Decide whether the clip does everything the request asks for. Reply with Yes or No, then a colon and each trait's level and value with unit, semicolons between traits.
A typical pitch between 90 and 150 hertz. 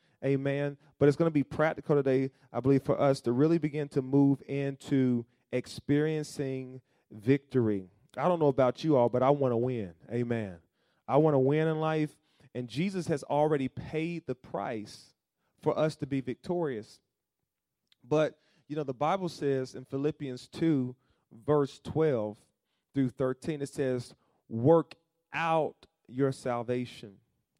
Yes: medium, 140 Hz